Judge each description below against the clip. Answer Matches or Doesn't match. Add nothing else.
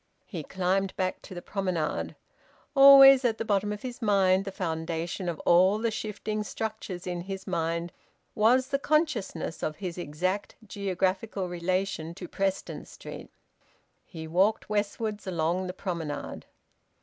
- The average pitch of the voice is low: Doesn't match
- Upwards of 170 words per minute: Doesn't match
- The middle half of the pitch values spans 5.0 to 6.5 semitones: Doesn't match